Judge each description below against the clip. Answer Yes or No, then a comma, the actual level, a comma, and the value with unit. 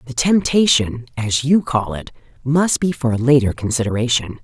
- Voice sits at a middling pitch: No, low, 130 Hz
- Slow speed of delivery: No, average, 160 wpm